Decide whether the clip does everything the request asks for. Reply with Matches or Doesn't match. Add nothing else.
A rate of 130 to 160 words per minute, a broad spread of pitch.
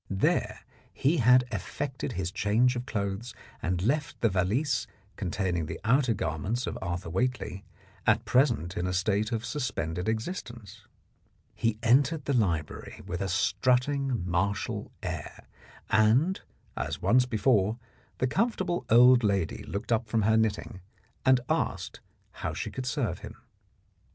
Doesn't match